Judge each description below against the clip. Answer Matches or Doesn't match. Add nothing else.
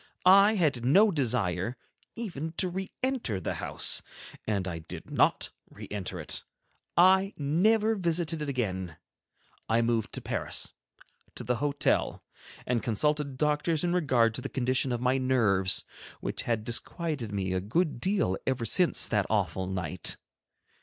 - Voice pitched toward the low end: Matches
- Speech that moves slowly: Doesn't match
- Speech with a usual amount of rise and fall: Doesn't match